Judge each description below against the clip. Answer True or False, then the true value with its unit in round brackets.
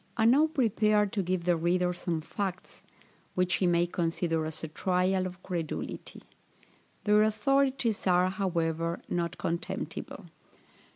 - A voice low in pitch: False (180 Hz)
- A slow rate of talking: True (130 wpm)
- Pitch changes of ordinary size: True (3.5 semitones)